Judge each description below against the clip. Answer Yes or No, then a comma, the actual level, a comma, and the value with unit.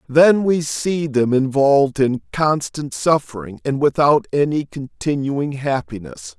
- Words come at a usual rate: No, slow, 120 wpm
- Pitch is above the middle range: No, medium, 140 Hz